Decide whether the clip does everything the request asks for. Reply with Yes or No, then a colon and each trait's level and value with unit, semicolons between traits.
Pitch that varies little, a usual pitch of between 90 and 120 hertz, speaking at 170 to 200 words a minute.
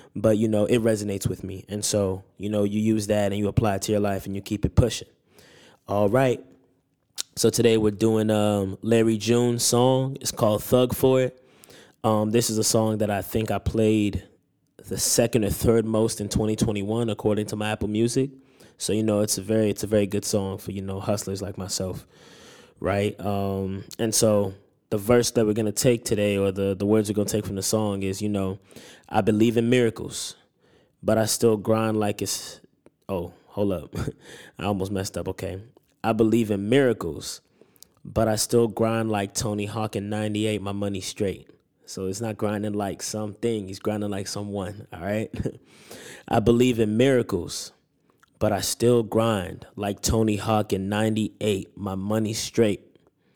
Yes: narrow, 2.1 semitones; low, 105 Hz; average, 185 wpm